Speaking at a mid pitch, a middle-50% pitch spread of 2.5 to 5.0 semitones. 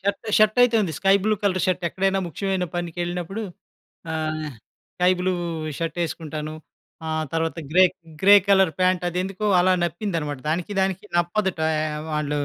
Yes: medium, 180 Hz; average, 3.2 semitones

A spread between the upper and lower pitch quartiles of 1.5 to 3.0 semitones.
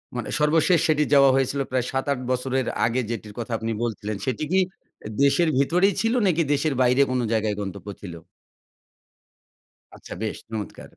No: average, 4.8 semitones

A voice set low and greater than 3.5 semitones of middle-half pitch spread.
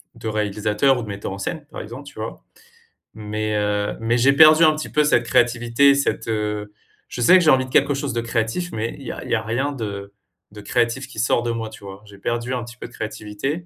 Yes: low, 115 Hz; average, 4.2 semitones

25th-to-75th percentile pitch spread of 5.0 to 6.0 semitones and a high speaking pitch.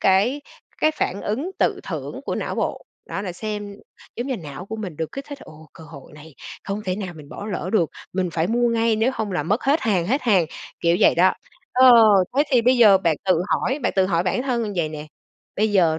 Yes: wide, 5.6 semitones; high, 200 Hz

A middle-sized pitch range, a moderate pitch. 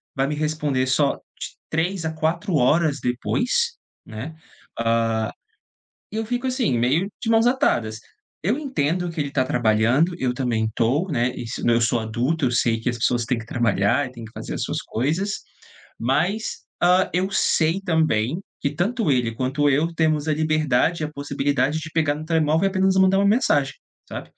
No: wide, 6.1 semitones; medium, 150 Hz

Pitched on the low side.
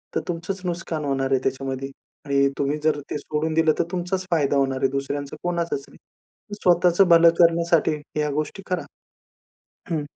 No: medium, 155 Hz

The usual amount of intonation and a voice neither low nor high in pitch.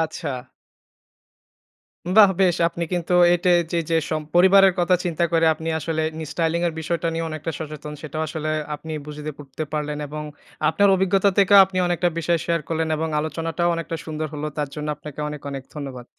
No: narrow, 2.3 semitones; medium, 160 Hz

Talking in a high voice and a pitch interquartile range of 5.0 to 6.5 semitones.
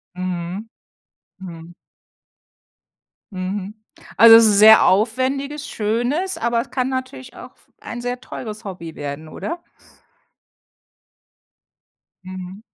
Yes: high, 215 Hz; wide, 5.4 semitones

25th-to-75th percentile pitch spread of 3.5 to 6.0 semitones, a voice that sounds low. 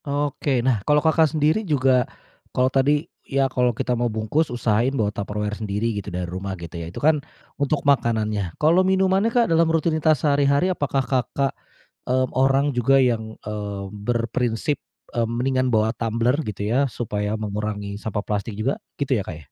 Yes: average, 5.0 semitones; low, 125 Hz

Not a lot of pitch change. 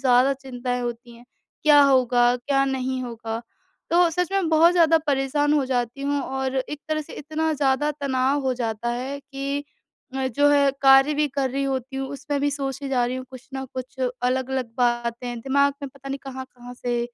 Yes: narrow, 2.2 semitones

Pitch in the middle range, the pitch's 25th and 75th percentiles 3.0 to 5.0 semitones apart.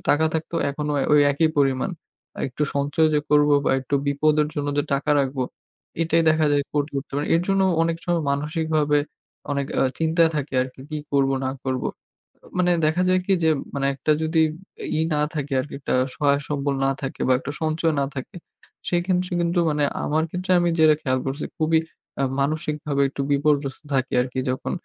No: medium, 150 Hz; narrow, 2.4 semitones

